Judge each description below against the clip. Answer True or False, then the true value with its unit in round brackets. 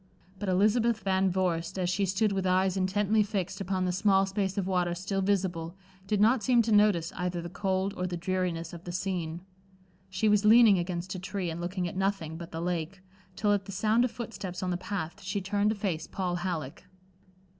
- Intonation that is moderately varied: False (2.3 semitones)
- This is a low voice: False (190 Hz)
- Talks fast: True (210 wpm)